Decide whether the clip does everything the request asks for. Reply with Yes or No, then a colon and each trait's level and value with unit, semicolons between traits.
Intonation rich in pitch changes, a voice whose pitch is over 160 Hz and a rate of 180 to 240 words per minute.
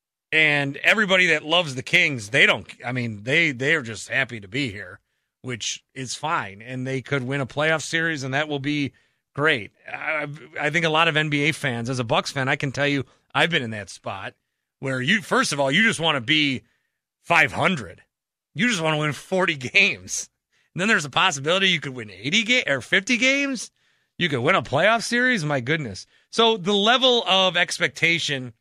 No: wide, 5.7 semitones; medium, 150 Hz; fast, 205 wpm